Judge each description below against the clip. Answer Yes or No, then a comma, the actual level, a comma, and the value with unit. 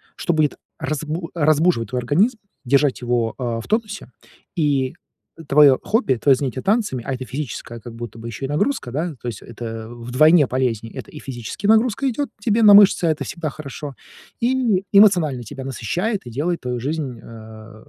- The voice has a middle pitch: Yes, medium, 145 Hz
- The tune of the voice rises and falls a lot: Yes, wide, 6.8 semitones